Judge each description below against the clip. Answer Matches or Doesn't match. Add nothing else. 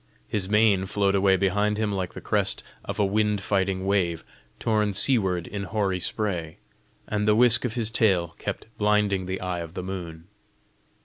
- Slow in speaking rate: Doesn't match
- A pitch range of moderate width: Doesn't match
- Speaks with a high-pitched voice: Doesn't match